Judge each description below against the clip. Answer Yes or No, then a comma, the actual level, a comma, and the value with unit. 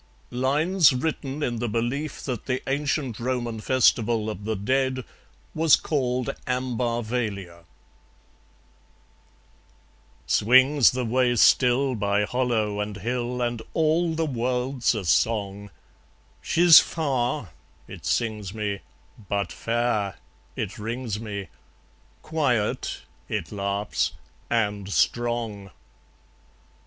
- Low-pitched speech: Yes, low, 120 Hz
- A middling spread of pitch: Yes, average, 3.6 semitones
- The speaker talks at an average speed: No, slow, 100 wpm